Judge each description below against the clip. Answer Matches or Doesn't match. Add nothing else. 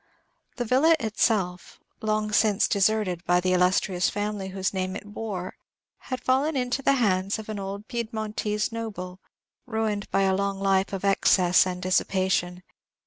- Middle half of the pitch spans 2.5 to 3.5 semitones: Matches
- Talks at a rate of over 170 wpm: Doesn't match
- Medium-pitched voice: Doesn't match